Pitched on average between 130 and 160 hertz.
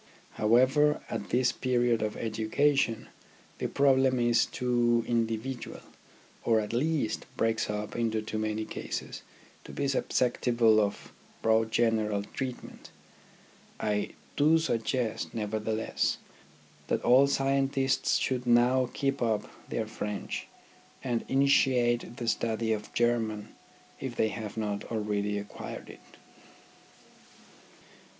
No: low, 115 Hz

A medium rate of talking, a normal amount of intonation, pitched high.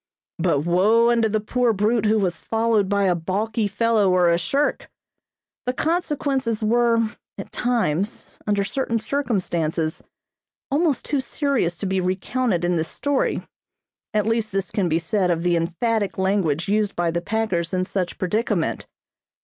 Yes: average, 155 wpm; average, 4.5 semitones; high, 205 Hz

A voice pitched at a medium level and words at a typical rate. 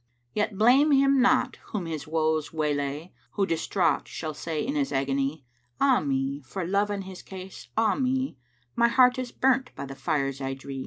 Yes: medium, 180 Hz; average, 190 wpm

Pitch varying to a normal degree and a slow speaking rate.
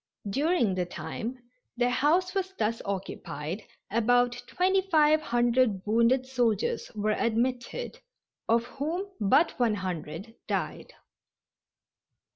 No: wide, 6.2 semitones; slow, 105 wpm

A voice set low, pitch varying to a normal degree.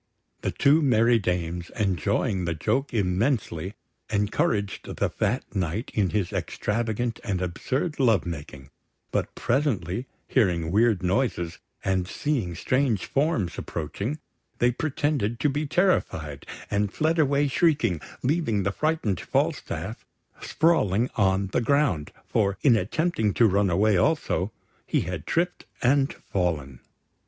No: low, 105 Hz; wide, 7.1 semitones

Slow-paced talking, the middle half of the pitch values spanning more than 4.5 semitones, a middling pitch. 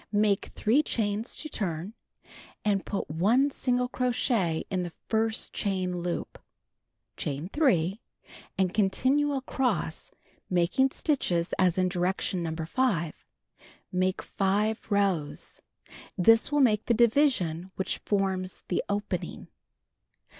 No: slow, 115 wpm; average, 5.0 semitones; high, 200 Hz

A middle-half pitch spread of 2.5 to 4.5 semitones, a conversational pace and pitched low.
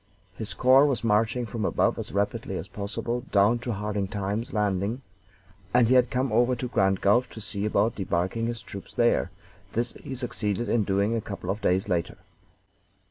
Yes: average, 3.2 semitones; average, 185 wpm; low, 110 Hz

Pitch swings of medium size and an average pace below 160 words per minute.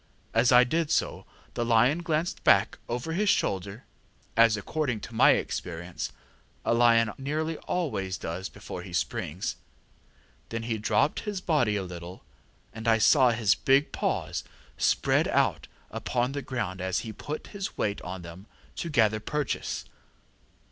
No: wide, 6.3 semitones; average, 150 wpm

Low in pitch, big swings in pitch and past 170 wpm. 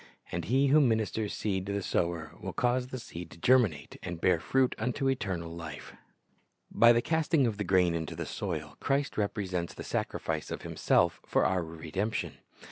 Yes: low, 100 Hz; wide, 6.6 semitones; average, 185 wpm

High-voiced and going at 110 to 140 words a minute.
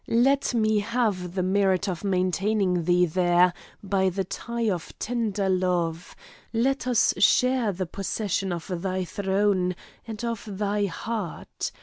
Yes: high, 195 Hz; slow, 135 wpm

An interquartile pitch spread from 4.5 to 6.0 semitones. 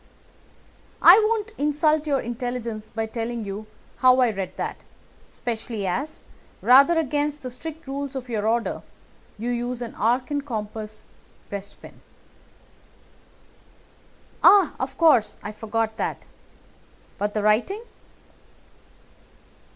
Yes: average, 4.8 semitones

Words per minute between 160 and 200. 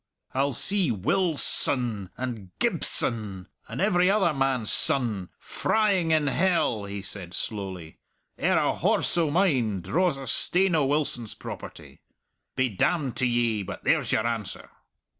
No: average, 145 wpm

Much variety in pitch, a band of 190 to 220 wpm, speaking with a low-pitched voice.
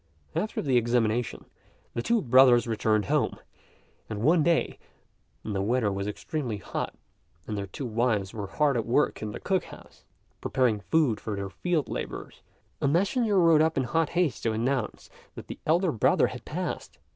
No: wide, 6.5 semitones; average, 175 wpm; low, 125 Hz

